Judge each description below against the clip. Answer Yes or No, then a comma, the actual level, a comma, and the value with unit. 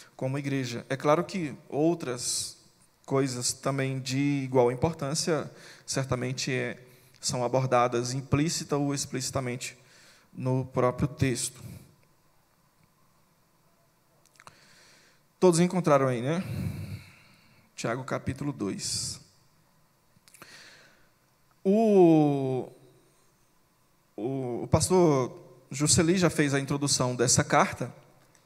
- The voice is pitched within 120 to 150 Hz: Yes, medium, 140 Hz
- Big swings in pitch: No, average, 4.5 semitones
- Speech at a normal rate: No, slow, 80 wpm